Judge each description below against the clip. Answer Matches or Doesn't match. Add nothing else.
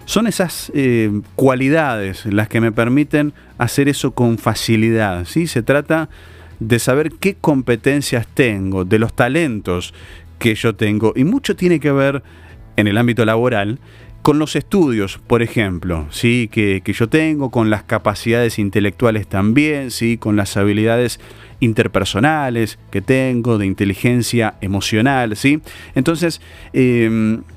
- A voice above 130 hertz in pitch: Doesn't match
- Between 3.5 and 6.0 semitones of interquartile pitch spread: Matches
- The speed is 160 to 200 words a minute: Doesn't match